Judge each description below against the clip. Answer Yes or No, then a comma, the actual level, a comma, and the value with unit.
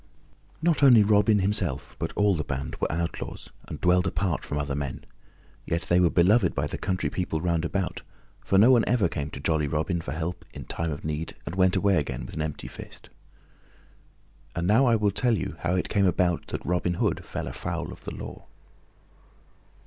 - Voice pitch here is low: Yes, very low, 90 Hz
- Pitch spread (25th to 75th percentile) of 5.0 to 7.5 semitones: No, average, 4.1 semitones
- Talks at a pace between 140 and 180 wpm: No, average, 195 wpm